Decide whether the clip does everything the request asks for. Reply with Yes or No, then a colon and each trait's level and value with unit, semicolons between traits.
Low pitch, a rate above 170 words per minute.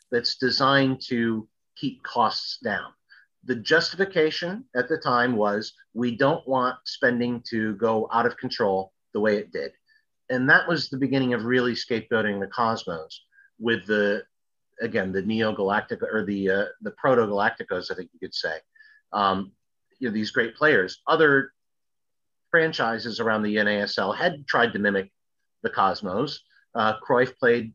No: low, 120 Hz; average, 150 wpm